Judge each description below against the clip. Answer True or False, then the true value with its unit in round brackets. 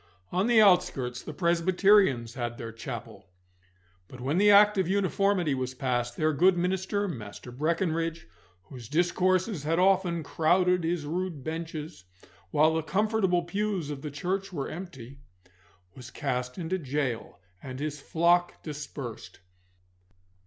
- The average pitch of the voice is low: False (165 Hz)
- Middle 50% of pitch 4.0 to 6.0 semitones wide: True (5.4 semitones)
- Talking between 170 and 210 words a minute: False (135 wpm)